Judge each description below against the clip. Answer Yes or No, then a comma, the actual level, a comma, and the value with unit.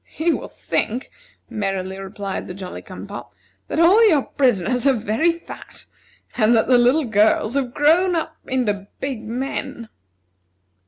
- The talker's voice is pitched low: No, high, 245 Hz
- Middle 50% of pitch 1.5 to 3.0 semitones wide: No, average, 5.3 semitones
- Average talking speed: Yes, average, 150 wpm